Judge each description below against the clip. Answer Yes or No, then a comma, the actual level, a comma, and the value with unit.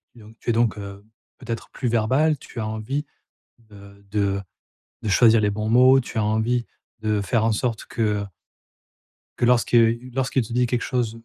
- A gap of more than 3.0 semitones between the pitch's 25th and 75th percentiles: No, narrow, 2.5 semitones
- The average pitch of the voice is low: Yes, low, 115 Hz